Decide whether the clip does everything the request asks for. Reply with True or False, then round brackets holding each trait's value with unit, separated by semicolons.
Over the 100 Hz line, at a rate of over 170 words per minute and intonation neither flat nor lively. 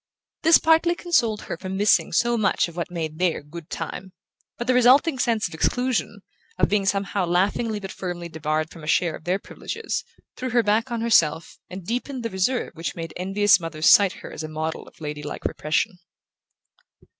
False (190 Hz; 190 wpm; 6.1 semitones)